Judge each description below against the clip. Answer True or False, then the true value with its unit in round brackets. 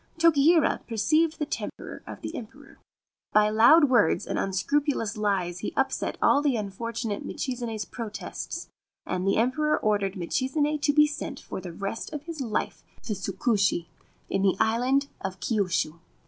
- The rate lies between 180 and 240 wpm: False (155 wpm)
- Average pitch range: False (6.5 semitones)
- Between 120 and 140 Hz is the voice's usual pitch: False (230 Hz)